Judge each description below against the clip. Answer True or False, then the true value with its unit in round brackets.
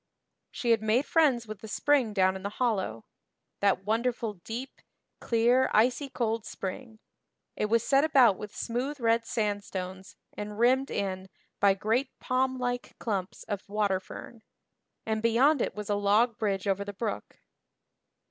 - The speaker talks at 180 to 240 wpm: False (155 wpm)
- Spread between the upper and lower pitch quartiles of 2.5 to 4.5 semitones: True (3.4 semitones)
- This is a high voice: True (220 Hz)